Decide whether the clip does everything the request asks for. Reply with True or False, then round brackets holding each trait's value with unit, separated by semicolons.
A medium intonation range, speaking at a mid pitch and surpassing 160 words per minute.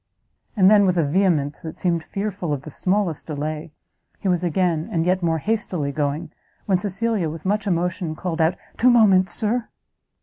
True (3.8 semitones; 180 Hz; 175 wpm)